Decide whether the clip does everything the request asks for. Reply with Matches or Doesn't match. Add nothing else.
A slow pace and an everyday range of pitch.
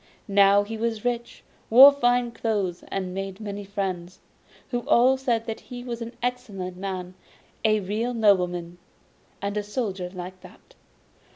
Doesn't match